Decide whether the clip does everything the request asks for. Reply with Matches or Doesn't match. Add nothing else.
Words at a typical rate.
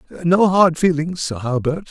Matches